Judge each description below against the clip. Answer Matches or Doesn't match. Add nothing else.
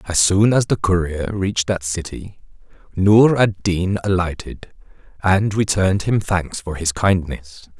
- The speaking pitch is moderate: Doesn't match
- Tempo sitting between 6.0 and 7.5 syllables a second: Doesn't match